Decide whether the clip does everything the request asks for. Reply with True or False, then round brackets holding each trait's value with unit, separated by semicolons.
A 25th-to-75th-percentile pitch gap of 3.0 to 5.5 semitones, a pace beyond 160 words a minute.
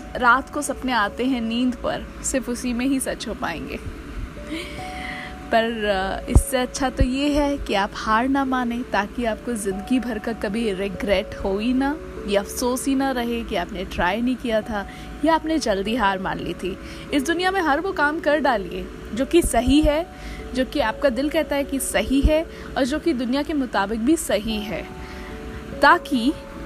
True (4.3 semitones; 190 wpm)